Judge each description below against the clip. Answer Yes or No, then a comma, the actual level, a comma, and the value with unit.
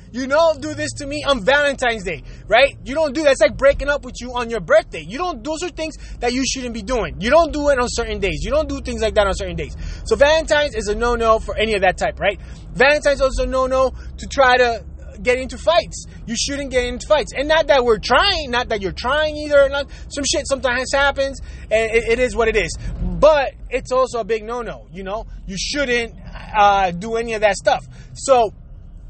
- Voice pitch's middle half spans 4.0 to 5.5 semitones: Yes, average, 4.3 semitones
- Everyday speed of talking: No, fast, 235 wpm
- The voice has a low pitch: No, very high, 250 Hz